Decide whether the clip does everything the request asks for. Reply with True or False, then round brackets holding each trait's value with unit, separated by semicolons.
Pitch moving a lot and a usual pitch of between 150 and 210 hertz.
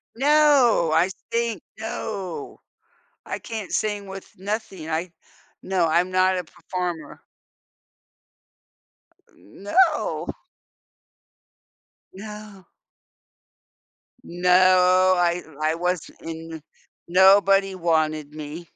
False (3.1 semitones; 185 Hz)